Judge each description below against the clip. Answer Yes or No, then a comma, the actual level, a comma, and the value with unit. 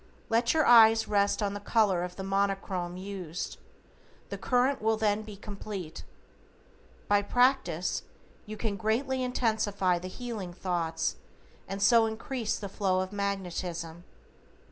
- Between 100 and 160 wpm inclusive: Yes, slow, 135 wpm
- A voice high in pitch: Yes, high, 200 Hz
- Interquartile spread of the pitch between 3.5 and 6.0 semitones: No, average, 3.1 semitones